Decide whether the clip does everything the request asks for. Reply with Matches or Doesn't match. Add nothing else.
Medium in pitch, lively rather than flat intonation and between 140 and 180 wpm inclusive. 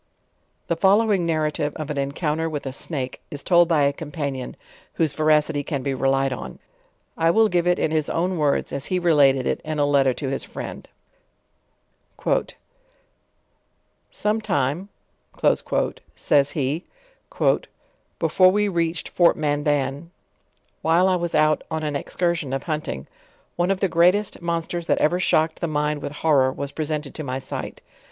Doesn't match